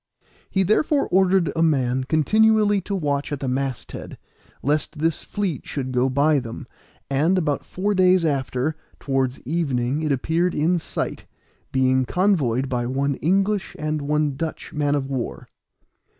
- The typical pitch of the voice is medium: Yes, medium, 150 Hz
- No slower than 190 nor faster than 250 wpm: No, average, 150 wpm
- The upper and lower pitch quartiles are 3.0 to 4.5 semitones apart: No, average, 5.2 semitones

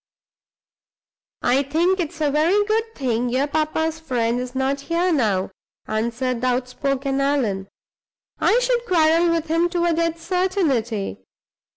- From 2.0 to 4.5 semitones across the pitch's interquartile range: No, average, 5.2 semitones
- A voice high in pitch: Yes, very high, 290 Hz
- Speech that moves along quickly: No, average, 140 wpm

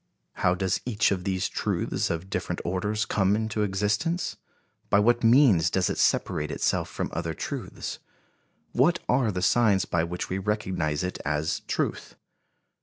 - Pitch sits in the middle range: No, low, 100 Hz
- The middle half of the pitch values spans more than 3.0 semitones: Yes, average, 3.4 semitones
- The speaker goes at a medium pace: Yes, average, 155 wpm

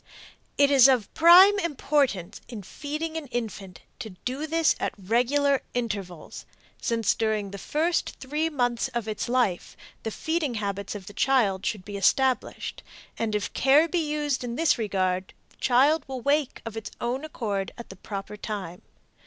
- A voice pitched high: Yes, high, 240 Hz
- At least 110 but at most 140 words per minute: No, average, 165 wpm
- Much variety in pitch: Yes, wide, 5.9 semitones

